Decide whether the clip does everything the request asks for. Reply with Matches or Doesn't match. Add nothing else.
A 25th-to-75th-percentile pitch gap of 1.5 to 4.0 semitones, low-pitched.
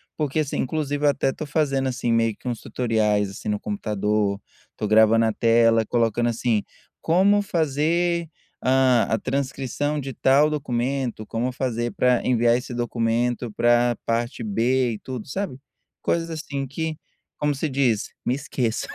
Matches